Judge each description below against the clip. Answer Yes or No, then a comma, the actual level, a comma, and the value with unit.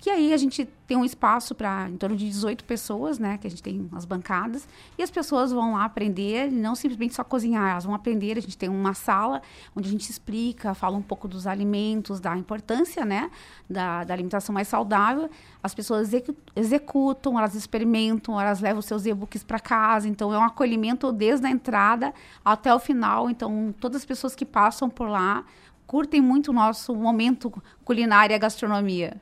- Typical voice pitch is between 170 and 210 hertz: No, high, 220 Hz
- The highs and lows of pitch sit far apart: No, average, 3.7 semitones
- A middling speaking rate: No, fast, 195 wpm